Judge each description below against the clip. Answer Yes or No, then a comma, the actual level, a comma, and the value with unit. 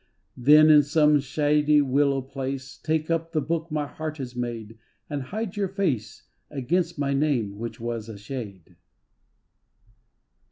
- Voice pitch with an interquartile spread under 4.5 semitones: Yes, average, 3.9 semitones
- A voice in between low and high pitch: Yes, medium, 145 Hz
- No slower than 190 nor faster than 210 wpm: No, average, 145 wpm